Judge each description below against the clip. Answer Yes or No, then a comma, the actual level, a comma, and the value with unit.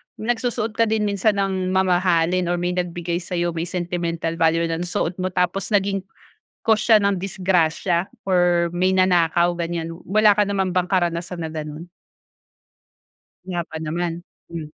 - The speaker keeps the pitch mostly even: Yes, narrow, 2.2 semitones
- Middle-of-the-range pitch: Yes, medium, 180 Hz